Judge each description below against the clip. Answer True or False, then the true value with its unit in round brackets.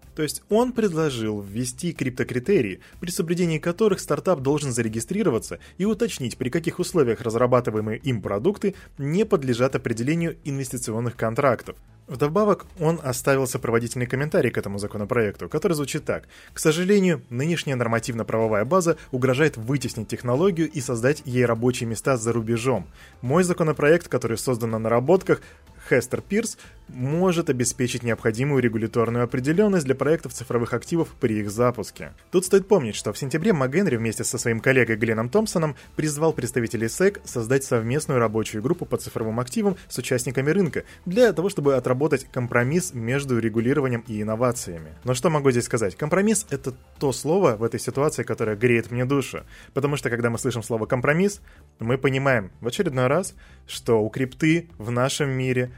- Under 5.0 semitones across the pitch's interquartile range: False (5.3 semitones)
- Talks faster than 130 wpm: True (150 wpm)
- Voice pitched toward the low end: True (130 Hz)